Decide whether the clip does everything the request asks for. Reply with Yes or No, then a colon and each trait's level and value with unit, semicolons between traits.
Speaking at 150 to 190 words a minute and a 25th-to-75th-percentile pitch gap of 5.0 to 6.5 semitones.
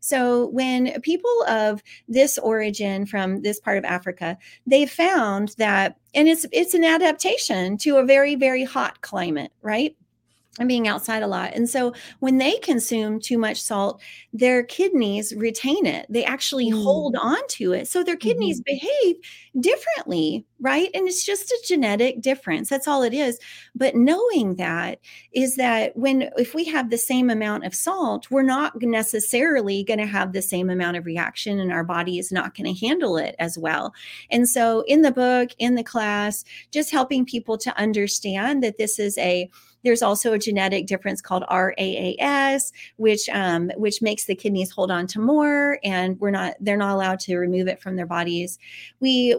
Yes: average, 180 wpm; wide, 5.5 semitones